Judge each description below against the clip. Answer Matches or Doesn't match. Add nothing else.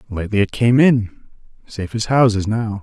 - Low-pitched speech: Matches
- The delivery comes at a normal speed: Matches